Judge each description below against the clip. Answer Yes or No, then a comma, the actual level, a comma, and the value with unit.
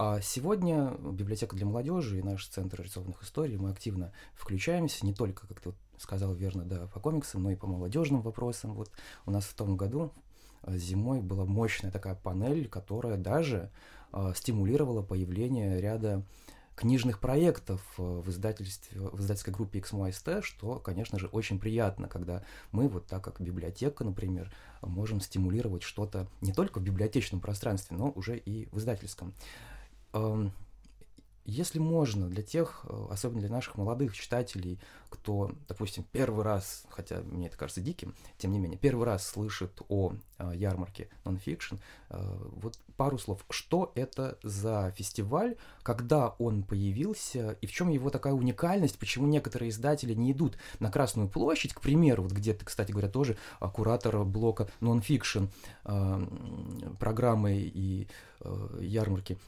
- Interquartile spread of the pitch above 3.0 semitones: Yes, average, 4.0 semitones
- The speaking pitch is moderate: No, low, 105 Hz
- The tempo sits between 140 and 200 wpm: Yes, average, 145 wpm